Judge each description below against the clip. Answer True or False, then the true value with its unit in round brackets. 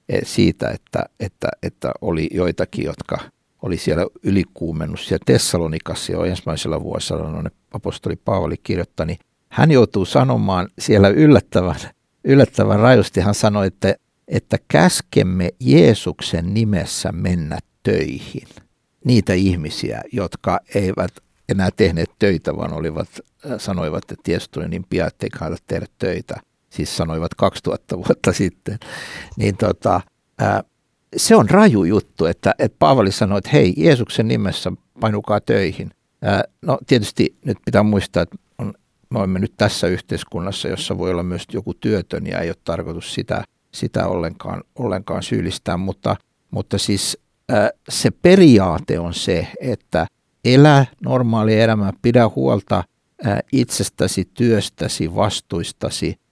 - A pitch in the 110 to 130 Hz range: False (100 Hz)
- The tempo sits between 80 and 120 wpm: False (130 wpm)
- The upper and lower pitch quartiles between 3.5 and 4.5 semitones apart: True (3.9 semitones)